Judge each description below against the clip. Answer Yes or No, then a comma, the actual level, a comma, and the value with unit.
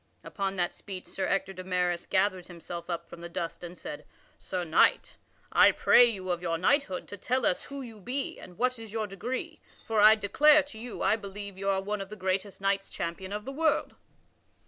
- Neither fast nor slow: No, fast, 215 wpm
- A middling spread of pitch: Yes, average, 3.4 semitones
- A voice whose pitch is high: Yes, high, 195 Hz